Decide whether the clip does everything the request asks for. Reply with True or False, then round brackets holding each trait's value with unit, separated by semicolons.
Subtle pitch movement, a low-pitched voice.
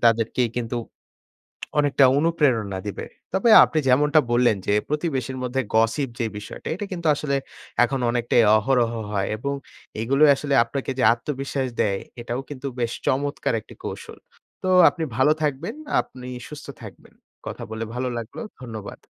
False (3.7 semitones; 130 Hz)